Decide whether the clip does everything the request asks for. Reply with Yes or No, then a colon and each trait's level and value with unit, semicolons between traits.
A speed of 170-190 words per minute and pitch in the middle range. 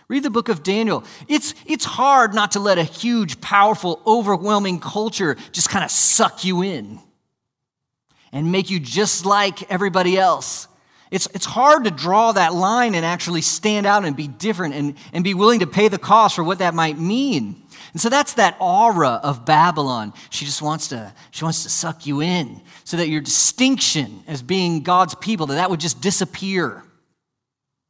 Yes: average, 185 wpm; medium, 180 Hz